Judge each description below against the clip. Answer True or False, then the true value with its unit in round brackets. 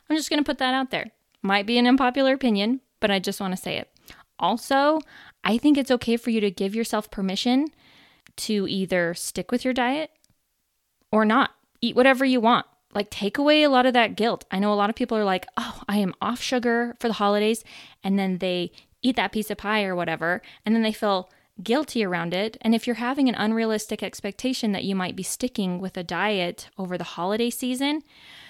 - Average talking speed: False (215 wpm)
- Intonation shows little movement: False (4.3 semitones)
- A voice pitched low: False (220 Hz)